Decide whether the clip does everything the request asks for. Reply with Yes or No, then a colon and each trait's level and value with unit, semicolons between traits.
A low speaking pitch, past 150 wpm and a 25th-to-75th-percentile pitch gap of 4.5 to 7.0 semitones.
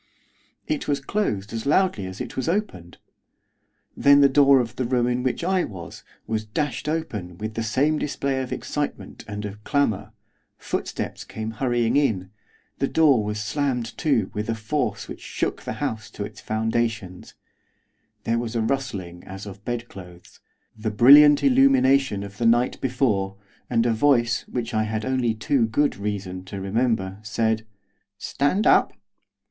Yes: low, 115 Hz; average, 165 wpm; average, 4.8 semitones